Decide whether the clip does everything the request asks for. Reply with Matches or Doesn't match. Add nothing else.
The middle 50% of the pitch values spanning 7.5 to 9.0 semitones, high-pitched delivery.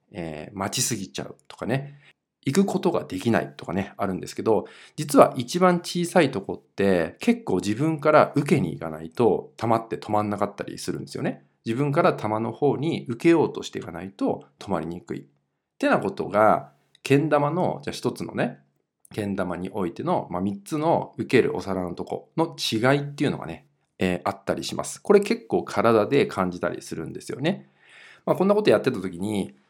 Doesn't match